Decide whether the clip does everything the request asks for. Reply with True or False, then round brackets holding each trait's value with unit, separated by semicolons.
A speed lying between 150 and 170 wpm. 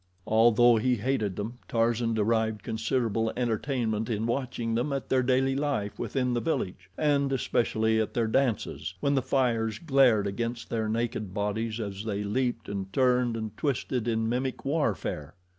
True (160 wpm)